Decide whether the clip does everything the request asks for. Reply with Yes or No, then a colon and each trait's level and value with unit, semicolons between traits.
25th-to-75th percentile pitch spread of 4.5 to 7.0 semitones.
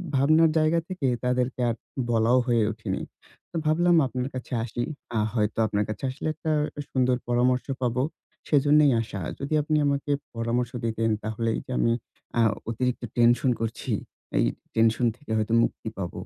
No: average, 3.5 semitones